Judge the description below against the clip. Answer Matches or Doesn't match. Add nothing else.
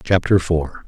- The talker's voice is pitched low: Matches